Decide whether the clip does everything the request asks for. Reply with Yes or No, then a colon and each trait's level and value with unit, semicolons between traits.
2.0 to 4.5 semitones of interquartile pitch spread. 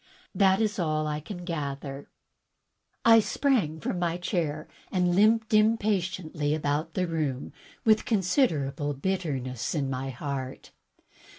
No: average, 5.0 semitones